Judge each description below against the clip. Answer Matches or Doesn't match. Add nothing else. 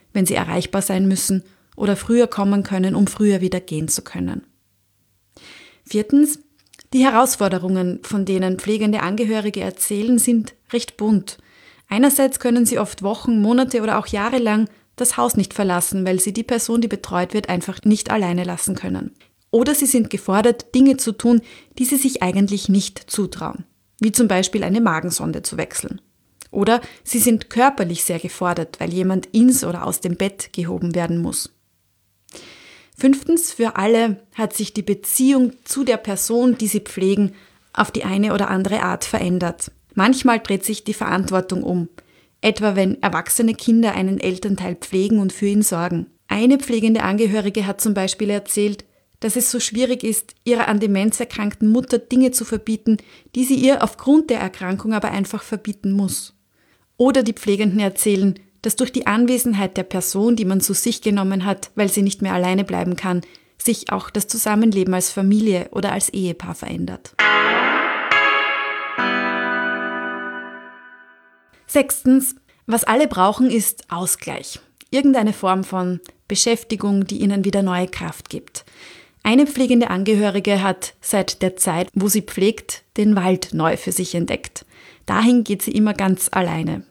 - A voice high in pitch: Matches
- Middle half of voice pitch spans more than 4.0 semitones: Doesn't match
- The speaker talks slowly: Doesn't match